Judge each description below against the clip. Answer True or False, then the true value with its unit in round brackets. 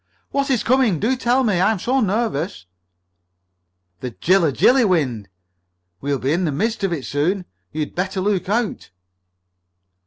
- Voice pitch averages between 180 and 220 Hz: True (190 Hz)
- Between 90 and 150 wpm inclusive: False (160 wpm)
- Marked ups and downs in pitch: True (7.2 semitones)